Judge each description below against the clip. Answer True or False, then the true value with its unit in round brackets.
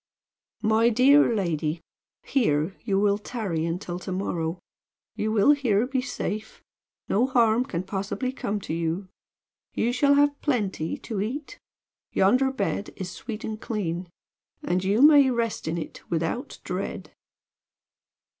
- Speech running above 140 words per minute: False (135 wpm)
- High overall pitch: True (210 Hz)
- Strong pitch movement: True (5.7 semitones)